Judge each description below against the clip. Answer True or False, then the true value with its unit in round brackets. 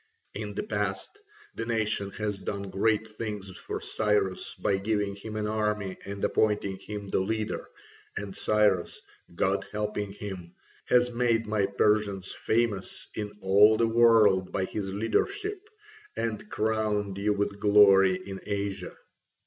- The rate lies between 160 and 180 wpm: False (140 wpm)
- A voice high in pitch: False (105 Hz)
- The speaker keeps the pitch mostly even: True (1.7 semitones)